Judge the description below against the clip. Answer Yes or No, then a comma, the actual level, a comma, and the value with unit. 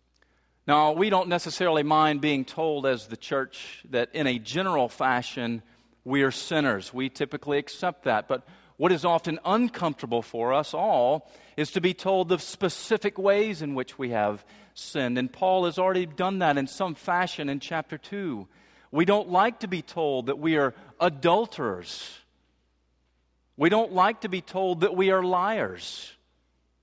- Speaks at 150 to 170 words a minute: Yes, average, 165 wpm